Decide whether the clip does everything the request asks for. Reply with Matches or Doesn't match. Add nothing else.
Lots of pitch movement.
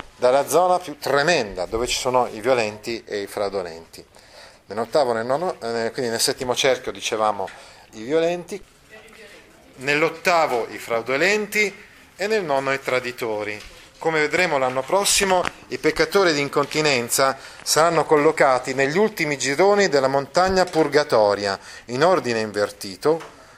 Matches